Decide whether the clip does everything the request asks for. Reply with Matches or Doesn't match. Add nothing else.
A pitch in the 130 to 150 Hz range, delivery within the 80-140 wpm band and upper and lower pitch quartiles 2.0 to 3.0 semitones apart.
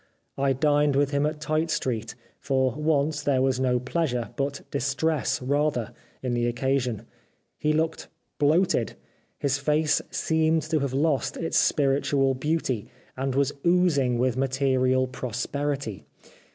Matches